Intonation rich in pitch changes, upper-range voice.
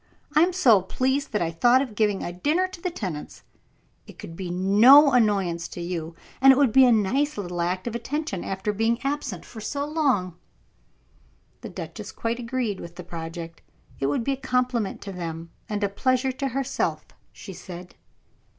Yes: wide, 6.7 semitones; high, 215 Hz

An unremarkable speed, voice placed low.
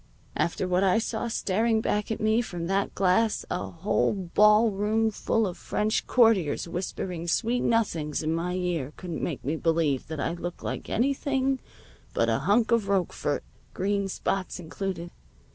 No: average, 160 wpm; high, 190 Hz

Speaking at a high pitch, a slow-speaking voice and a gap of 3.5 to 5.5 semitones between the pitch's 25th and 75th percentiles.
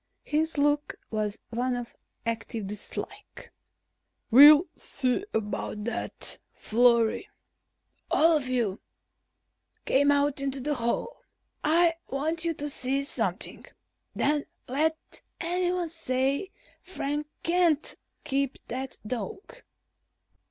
Yes: very high, 280 Hz; slow, 100 wpm; average, 4.5 semitones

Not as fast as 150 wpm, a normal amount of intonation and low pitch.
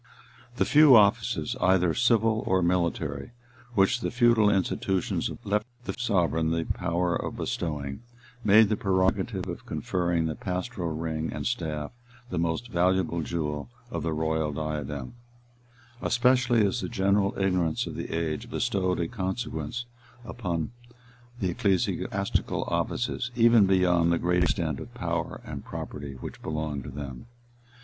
Yes: average, 140 wpm; average, 4.6 semitones; very low, 90 Hz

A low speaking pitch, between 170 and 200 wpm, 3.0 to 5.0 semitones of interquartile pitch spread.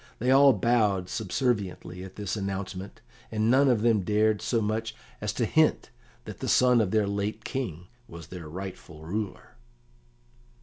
No: low, 105 Hz; average, 160 wpm; average, 3.4 semitones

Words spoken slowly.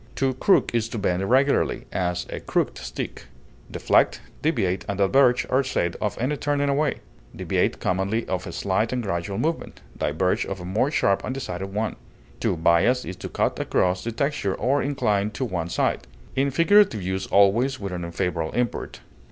No: average, 175 wpm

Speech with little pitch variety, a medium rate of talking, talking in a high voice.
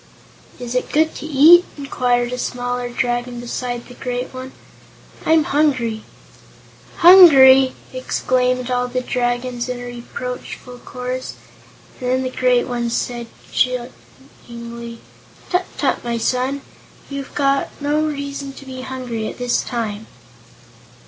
No: narrow, 1.6 semitones; slow, 125 wpm; very high, 250 Hz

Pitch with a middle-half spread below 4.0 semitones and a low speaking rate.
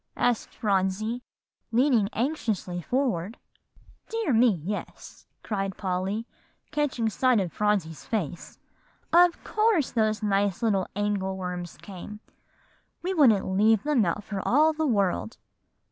No: average, 4.8 semitones; slow, 115 wpm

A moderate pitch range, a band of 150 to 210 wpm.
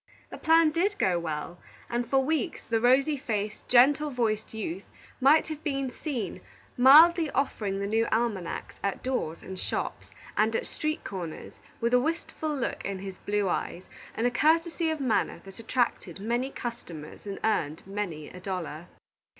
No: wide, 6.3 semitones; average, 165 wpm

